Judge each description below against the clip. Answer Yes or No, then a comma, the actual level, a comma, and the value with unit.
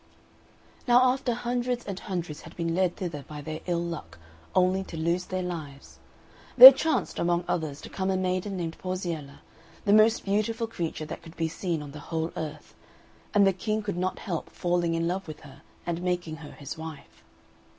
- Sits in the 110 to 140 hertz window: No, medium, 175 Hz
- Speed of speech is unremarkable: Yes, average, 190 wpm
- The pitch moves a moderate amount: Yes, average, 3.3 semitones